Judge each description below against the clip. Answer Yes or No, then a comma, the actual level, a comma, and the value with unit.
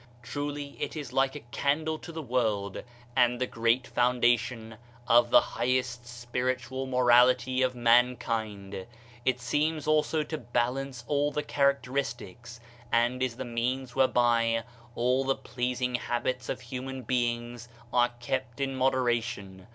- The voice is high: No, low, 125 Hz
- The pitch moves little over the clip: Yes, narrow, 1.8 semitones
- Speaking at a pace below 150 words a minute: Yes, slow, 135 wpm